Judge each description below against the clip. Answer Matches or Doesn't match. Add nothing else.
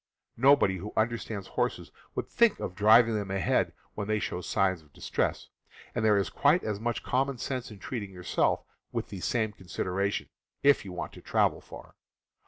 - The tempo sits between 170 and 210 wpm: Matches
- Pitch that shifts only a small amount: Doesn't match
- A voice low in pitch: Matches